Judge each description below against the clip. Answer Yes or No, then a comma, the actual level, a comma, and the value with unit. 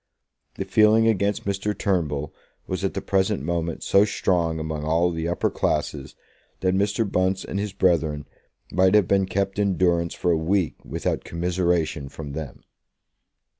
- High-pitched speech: No, very low, 90 Hz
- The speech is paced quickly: No, average, 160 wpm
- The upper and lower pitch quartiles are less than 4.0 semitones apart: Yes, average, 3.3 semitones